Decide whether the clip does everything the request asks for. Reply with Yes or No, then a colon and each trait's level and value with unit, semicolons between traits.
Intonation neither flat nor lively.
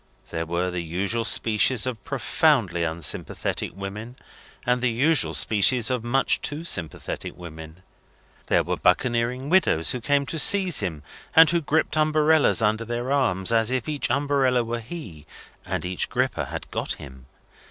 No: wide, 7.4 semitones